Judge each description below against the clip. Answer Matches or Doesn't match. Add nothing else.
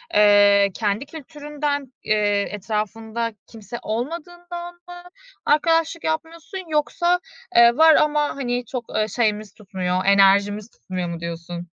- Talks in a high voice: Matches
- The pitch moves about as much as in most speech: Doesn't match